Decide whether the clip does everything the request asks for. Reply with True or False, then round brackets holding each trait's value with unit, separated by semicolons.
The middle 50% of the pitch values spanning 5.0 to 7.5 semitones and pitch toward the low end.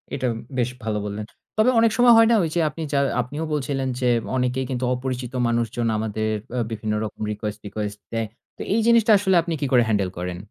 True (5.6 semitones; 125 Hz)